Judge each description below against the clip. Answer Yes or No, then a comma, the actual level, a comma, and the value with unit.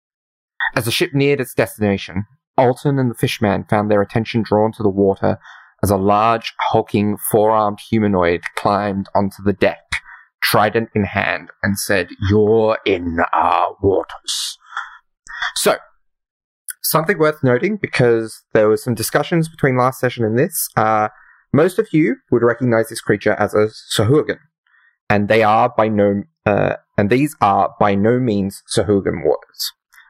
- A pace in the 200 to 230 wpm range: No, average, 150 wpm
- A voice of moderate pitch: No, low, 110 Hz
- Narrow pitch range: No, average, 3.5 semitones